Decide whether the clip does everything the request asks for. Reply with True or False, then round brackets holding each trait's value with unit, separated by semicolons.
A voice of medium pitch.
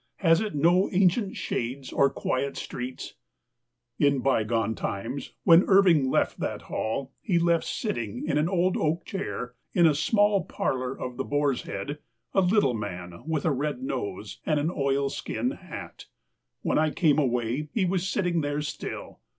True (145 Hz)